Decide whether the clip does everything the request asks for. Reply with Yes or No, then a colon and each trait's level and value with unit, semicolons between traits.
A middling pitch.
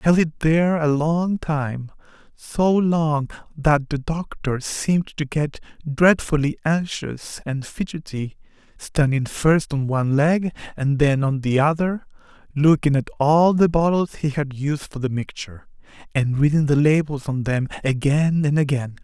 Yes: medium, 150 Hz